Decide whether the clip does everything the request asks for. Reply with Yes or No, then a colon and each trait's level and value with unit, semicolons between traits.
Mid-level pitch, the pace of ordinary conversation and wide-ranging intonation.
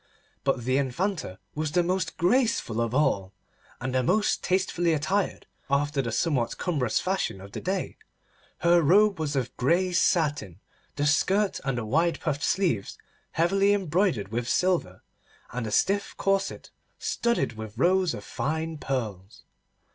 Yes: medium, 155 Hz; average, 145 wpm; wide, 7.1 semitones